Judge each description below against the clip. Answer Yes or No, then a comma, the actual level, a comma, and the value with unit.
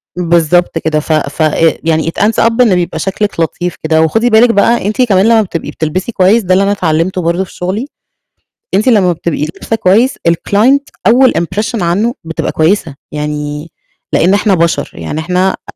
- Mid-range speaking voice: Yes, medium, 180 Hz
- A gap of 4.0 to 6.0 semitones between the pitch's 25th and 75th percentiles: Yes, average, 4.7 semitones